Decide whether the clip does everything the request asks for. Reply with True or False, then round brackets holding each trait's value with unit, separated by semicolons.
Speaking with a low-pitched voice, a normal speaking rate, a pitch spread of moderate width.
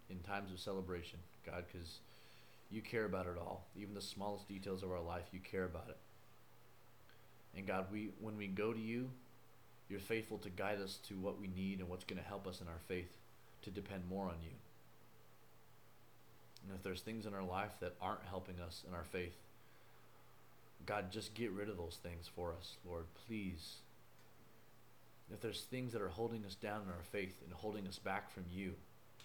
True (100 Hz; 195 wpm; 3.4 semitones)